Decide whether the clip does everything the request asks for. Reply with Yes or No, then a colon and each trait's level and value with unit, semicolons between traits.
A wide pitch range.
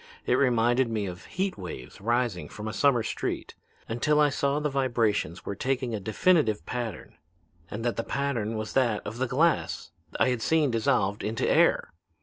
No: average, 3.9 semitones